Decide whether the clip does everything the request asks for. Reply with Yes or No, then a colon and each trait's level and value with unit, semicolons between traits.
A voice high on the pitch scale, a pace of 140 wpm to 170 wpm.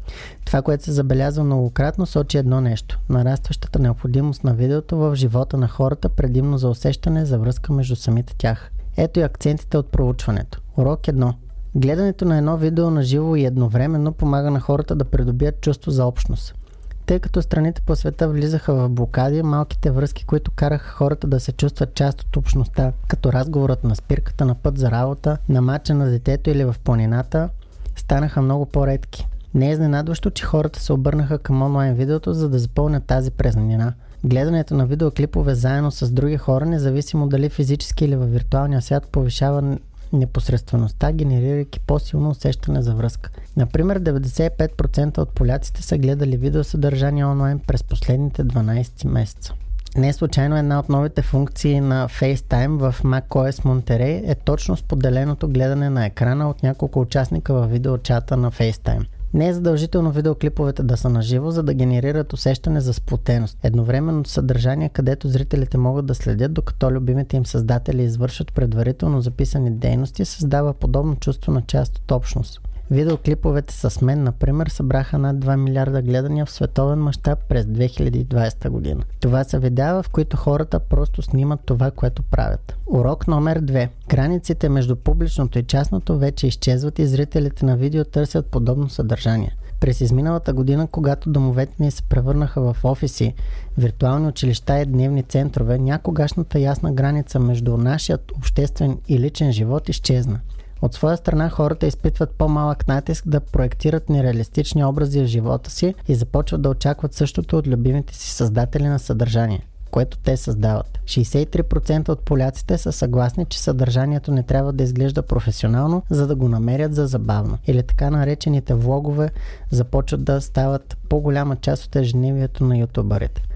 No: low, 135 Hz; average, 155 wpm